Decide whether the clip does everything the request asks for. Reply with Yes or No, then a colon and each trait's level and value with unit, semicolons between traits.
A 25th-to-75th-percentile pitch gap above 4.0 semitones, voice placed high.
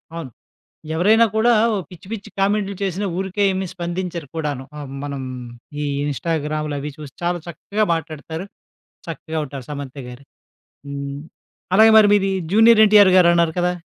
No: average, 4.9 semitones; medium, 170 Hz